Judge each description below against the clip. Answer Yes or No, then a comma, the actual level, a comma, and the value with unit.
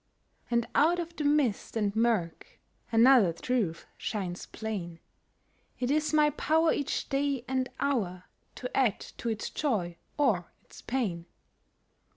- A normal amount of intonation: No, wide, 6.2 semitones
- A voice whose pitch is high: Yes, high, 235 Hz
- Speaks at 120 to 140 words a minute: Yes, slow, 135 wpm